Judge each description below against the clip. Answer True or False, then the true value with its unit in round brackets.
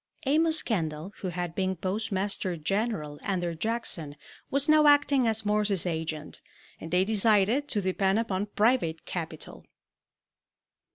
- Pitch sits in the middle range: False (195 Hz)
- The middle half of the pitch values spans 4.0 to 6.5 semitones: True (4.7 semitones)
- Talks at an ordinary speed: False (125 wpm)